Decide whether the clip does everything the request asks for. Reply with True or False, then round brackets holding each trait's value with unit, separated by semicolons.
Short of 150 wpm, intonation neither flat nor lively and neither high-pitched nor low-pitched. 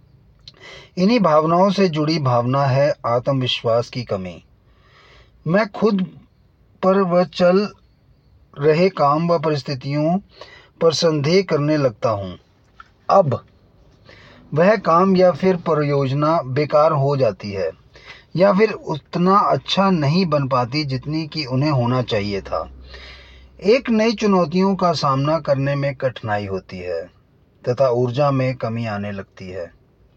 False (125 wpm; 6.3 semitones; 145 Hz)